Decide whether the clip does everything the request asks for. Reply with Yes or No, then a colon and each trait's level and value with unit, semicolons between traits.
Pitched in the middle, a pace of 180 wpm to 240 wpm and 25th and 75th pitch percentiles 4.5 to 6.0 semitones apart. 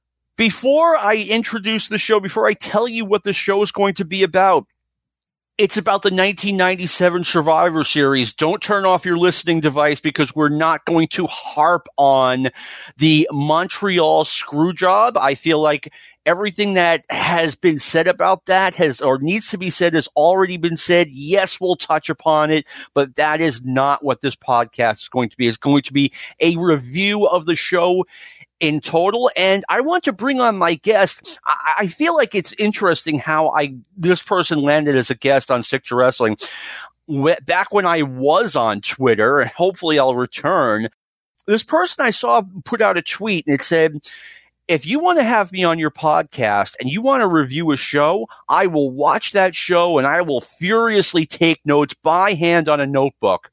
Yes: medium, 165 Hz; average, 185 wpm; average, 4.9 semitones